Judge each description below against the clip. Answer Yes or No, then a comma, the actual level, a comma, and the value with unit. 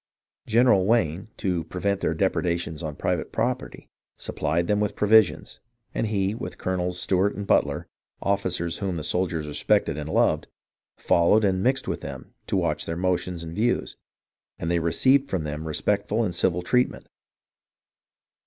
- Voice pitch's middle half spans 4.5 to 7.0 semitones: No, average, 3.7 semitones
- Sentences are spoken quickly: No, average, 155 wpm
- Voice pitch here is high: No, very low, 90 Hz